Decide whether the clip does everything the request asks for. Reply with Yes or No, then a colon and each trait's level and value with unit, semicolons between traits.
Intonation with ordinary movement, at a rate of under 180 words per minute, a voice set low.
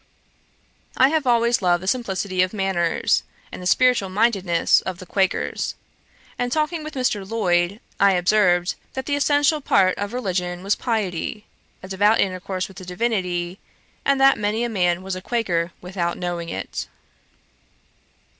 No: average, 4.7 semitones; average, 155 wpm; high, 195 Hz